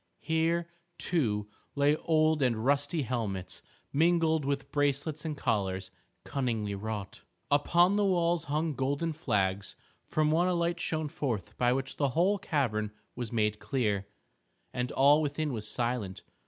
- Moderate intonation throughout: No, wide, 6.2 semitones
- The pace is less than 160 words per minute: Yes, average, 140 wpm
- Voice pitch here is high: No, medium, 140 Hz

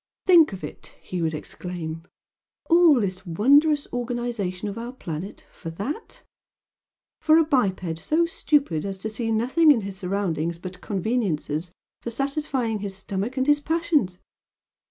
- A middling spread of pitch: No, wide, 7.6 semitones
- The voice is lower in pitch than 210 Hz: No, high, 215 Hz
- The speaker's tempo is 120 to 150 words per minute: Yes, average, 145 wpm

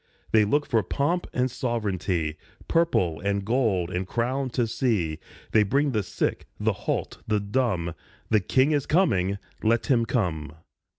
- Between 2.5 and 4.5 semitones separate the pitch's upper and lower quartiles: No, wide, 5.6 semitones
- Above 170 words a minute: No, average, 155 wpm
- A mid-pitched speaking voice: No, low, 110 Hz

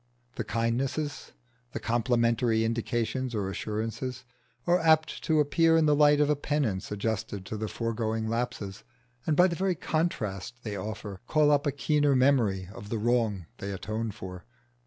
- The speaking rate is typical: Yes, average, 160 wpm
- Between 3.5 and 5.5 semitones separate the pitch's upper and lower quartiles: Yes, average, 5.2 semitones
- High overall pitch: No, low, 115 Hz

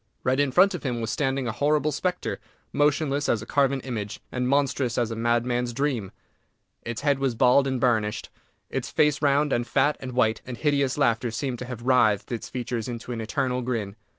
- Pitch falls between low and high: No, low, 125 Hz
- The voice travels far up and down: No, average, 3.0 semitones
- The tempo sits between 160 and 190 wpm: No, average, 200 wpm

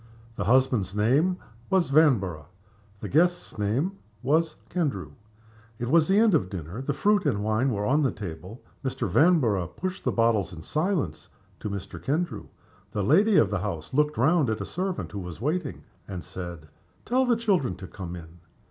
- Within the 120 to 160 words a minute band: No, average, 185 wpm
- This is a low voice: Yes, low, 125 Hz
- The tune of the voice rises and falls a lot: Yes, wide, 8.8 semitones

